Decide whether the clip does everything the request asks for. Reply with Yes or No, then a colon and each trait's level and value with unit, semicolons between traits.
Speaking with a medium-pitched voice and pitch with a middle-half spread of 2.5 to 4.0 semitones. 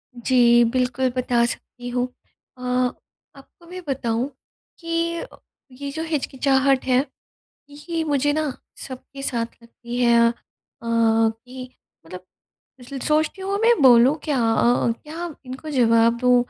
No: very high, 255 Hz; average, 3.7 semitones